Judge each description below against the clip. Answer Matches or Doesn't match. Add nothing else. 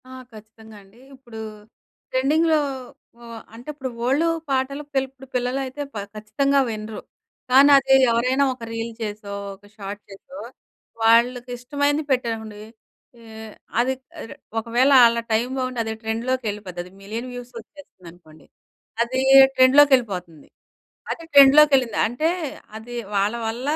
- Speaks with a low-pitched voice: Doesn't match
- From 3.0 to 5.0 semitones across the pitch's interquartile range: Matches